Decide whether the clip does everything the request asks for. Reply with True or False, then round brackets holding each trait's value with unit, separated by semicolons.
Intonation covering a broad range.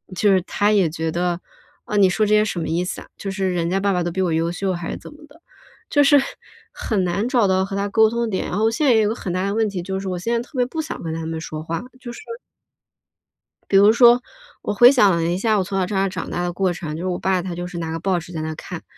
False (3.5 semitones)